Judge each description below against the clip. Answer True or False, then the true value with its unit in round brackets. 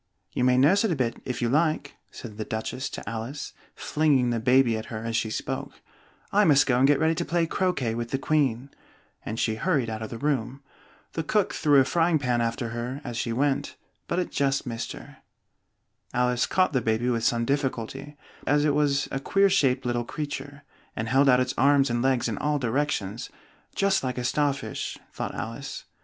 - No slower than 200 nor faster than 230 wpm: True (205 wpm)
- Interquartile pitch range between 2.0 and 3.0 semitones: False (3.7 semitones)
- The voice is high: False (130 Hz)